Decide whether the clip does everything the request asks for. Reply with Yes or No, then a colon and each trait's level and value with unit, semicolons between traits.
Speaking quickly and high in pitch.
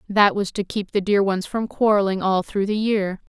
Yes: fast, 235 wpm; high, 200 Hz